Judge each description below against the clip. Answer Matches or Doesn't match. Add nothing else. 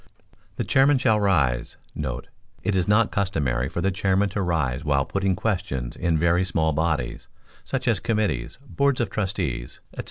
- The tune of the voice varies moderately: Doesn't match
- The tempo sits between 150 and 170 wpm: Matches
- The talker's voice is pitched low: Matches